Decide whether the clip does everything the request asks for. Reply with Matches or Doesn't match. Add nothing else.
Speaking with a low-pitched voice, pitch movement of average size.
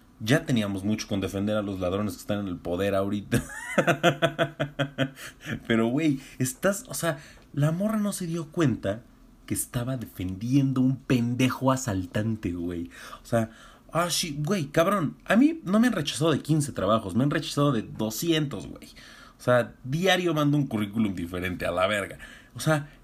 Doesn't match